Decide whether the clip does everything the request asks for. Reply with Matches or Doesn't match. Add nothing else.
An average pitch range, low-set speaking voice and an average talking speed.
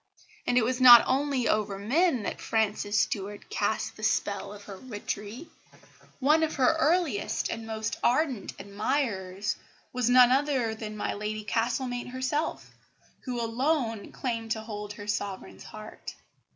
Doesn't match